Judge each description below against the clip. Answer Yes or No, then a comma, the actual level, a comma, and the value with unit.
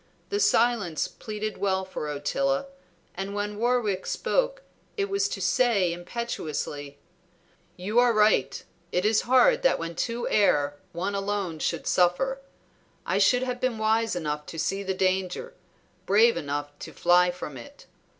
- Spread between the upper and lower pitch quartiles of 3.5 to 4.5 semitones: No, wide, 5.5 semitones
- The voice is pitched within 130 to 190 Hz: No, high, 205 Hz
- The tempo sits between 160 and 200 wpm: No, average, 150 wpm